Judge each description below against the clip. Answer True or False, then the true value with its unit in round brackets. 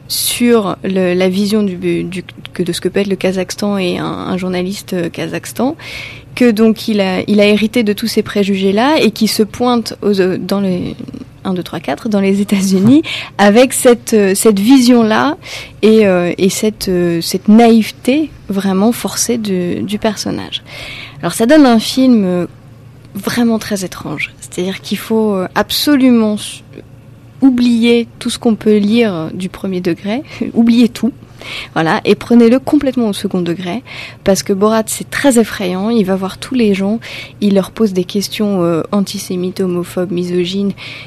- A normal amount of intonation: True (3.9 semitones)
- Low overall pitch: False (200 Hz)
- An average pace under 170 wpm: True (150 wpm)